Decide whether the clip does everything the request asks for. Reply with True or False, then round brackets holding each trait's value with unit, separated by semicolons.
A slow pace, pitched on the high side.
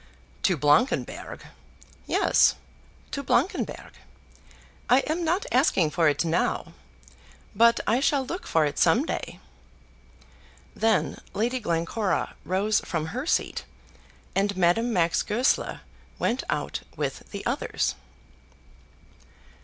True (110 wpm; 220 Hz)